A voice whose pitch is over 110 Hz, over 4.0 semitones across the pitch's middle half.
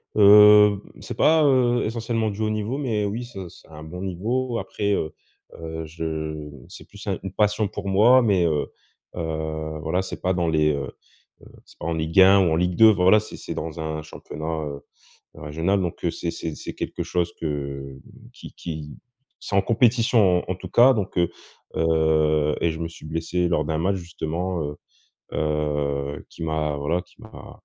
No: very low, 85 Hz; average, 4.8 semitones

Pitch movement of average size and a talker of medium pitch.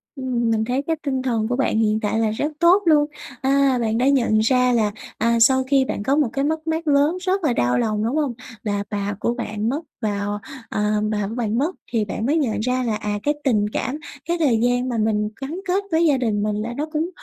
No: average, 4.7 semitones; high, 245 Hz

